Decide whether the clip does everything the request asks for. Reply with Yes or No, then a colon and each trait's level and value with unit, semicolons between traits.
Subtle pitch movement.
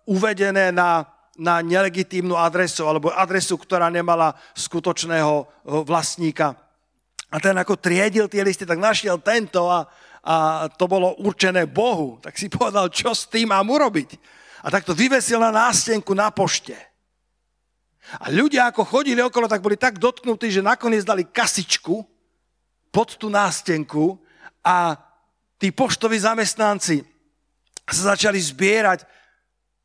No: average, 4.4 semitones